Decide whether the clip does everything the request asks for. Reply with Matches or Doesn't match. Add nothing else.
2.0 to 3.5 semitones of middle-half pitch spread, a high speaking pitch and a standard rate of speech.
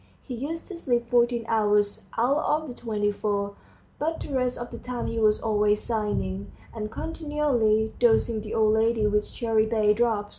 Matches